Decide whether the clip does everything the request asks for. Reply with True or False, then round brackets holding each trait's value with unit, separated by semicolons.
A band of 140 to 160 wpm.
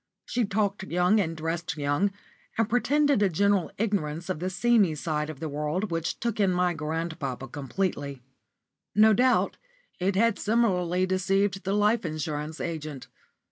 True (150 wpm)